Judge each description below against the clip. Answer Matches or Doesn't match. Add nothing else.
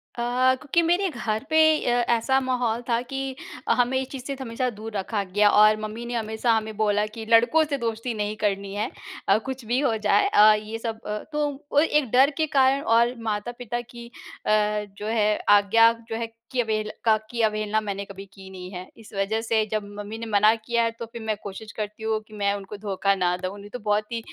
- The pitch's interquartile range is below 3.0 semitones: Matches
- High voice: Matches